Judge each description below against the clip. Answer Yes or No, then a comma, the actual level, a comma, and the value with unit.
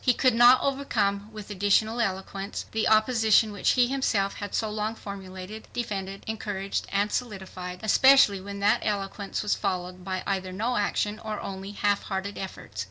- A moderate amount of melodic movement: No, narrow, 2.2 semitones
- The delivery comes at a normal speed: Yes, average, 165 wpm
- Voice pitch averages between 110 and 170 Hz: No, high, 205 Hz